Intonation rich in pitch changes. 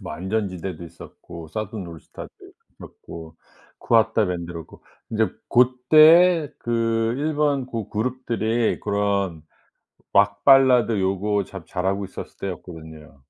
No: average, 5.0 semitones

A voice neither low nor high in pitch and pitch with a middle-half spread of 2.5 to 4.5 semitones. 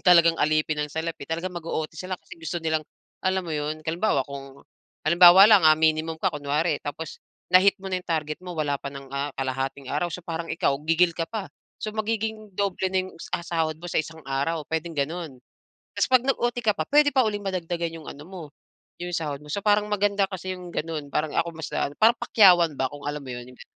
Yes: medium, 165 Hz; average, 3.6 semitones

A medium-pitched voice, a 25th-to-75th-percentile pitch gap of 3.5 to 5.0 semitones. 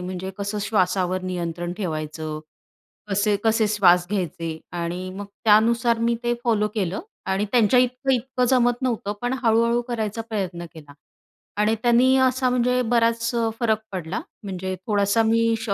No: high, 210 Hz; average, 4.2 semitones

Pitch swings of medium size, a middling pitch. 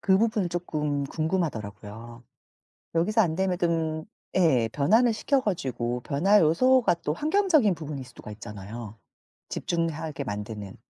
No: wide, 7.9 semitones; medium, 160 Hz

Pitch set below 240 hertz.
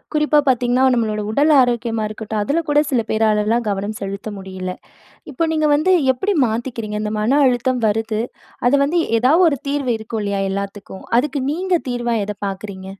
Yes: high, 230 Hz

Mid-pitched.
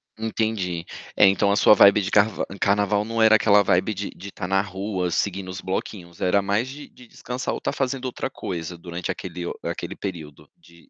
No: low, 100 Hz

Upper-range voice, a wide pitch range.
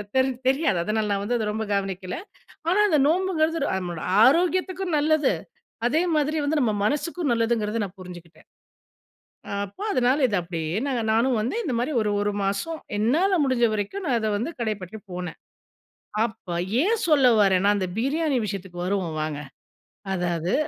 Yes: high, 225 Hz; wide, 7.6 semitones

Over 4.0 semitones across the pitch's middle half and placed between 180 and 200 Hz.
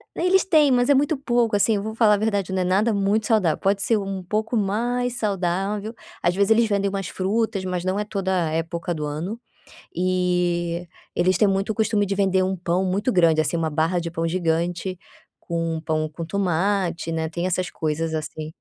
No: average, 3.7 semitones; high, 190 Hz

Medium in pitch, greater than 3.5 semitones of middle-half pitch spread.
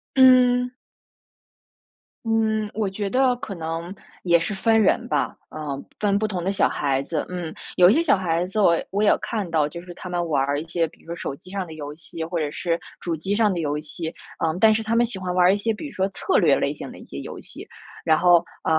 Yes: medium, 180 Hz; average, 4.8 semitones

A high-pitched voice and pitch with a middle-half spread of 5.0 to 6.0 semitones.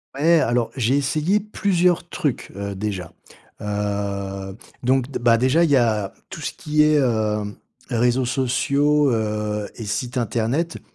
No: low, 120 Hz; wide, 5.6 semitones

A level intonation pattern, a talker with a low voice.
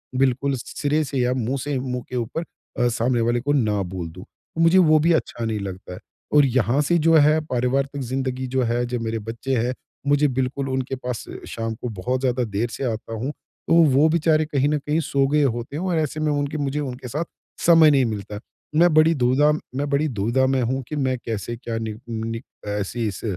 No: average, 3.6 semitones; low, 130 Hz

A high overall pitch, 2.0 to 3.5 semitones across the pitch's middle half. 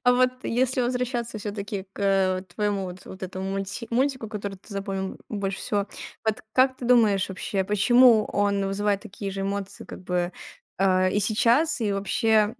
Yes: high, 205 Hz; average, 3.0 semitones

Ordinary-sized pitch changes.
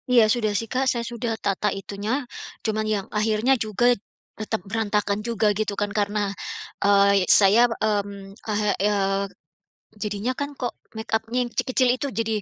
No: narrow, 2.1 semitones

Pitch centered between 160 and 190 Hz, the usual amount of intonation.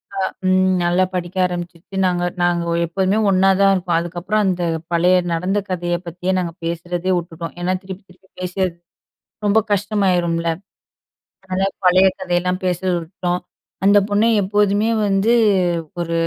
No: medium, 185 Hz; narrow, 1.7 semitones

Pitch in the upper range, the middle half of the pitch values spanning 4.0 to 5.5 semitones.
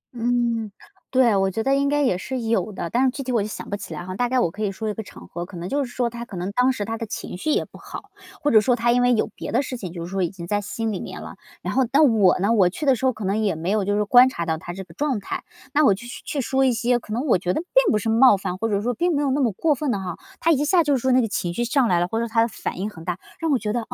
Yes: high, 230 Hz; average, 4.8 semitones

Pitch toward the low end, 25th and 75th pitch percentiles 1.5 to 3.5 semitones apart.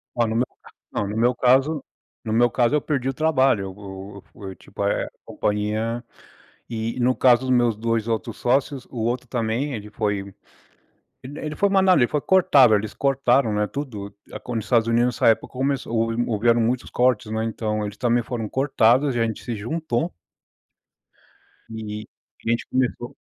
Yes: low, 120 Hz; average, 2.9 semitones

